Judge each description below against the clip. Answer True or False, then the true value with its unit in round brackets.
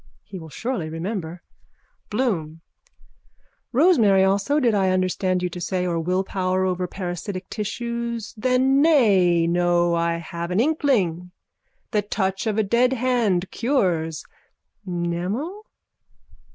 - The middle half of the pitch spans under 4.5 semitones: False (5.2 semitones)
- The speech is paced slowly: True (120 wpm)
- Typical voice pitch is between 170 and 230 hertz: True (190 Hz)